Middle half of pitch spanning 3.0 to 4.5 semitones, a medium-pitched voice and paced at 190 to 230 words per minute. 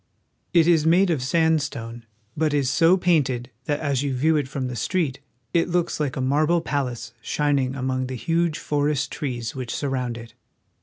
No: average, 3.9 semitones; medium, 145 Hz; average, 175 wpm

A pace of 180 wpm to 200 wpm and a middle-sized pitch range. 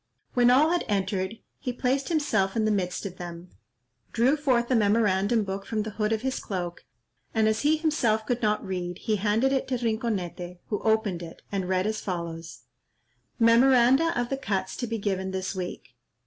Yes: average, 190 wpm; average, 4.3 semitones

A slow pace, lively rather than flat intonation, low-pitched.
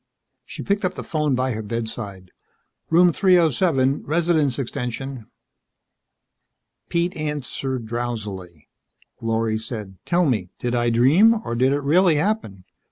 Yes: slow, 125 wpm; wide, 6.2 semitones; low, 130 Hz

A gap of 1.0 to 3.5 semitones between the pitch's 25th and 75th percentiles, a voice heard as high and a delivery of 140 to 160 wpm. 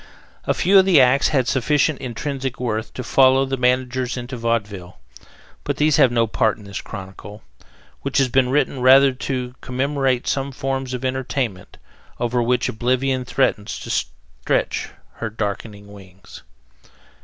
No: average, 3.0 semitones; low, 125 Hz; average, 150 wpm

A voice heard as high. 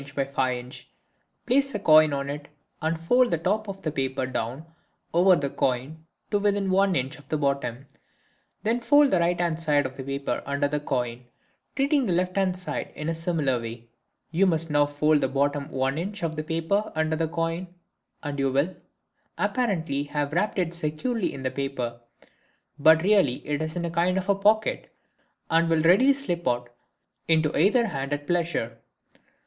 No: medium, 160 Hz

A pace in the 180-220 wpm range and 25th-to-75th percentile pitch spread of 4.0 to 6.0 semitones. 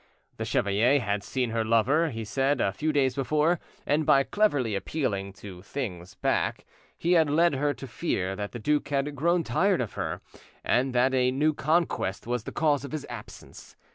Yes: average, 190 wpm; average, 5.1 semitones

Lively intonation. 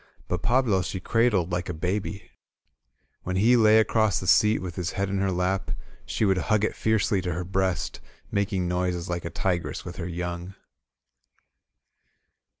No: average, 2.7 semitones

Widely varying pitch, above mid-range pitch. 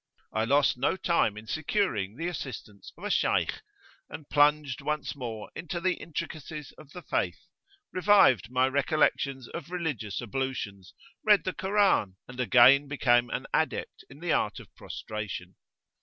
No: wide, 5.8 semitones; medium, 140 Hz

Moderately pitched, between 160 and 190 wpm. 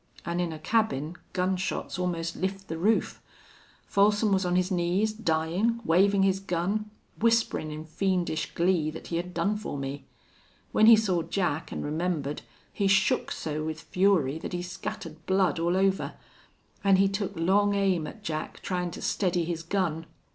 Yes: medium, 180 Hz; average, 170 wpm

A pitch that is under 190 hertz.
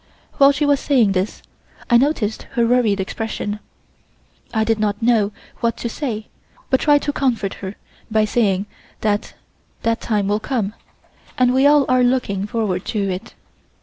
No: high, 225 Hz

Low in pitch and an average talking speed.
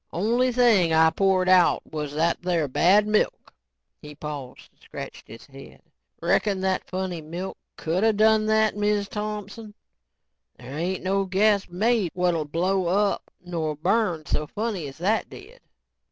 No: medium, 185 Hz; average, 150 wpm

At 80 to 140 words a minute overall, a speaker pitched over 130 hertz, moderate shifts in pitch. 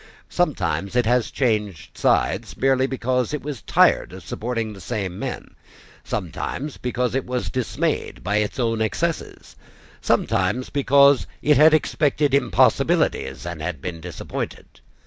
No: slow, 135 wpm; low, 120 Hz; average, 5.0 semitones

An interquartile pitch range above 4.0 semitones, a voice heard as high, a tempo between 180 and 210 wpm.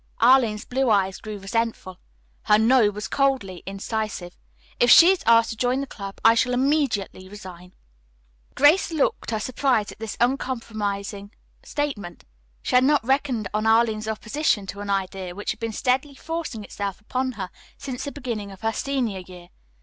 No: average, 4.4 semitones; high, 220 Hz; average, 165 wpm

